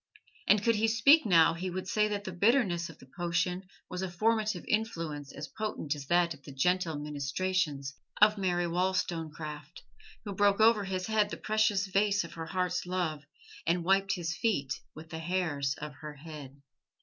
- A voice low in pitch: No, medium, 180 Hz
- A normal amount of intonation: Yes, average, 4.4 semitones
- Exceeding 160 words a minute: Yes, average, 180 wpm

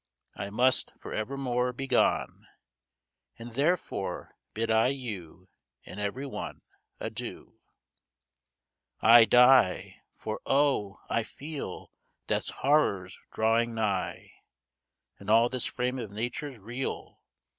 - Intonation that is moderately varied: Yes, average, 3.5 semitones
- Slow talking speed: Yes, slow, 110 wpm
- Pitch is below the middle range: Yes, low, 120 Hz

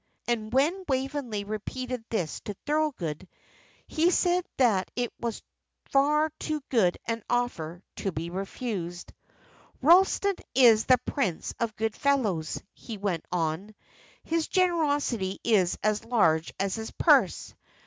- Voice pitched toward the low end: No, high, 230 Hz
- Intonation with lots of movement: Yes, wide, 6.6 semitones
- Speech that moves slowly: Yes, slow, 130 wpm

